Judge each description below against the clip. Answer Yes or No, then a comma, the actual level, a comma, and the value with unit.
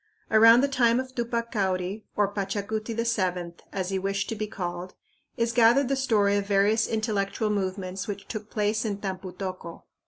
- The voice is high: Yes, high, 205 Hz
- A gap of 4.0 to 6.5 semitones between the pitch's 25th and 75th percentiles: No, average, 2.9 semitones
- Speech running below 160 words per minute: No, average, 175 wpm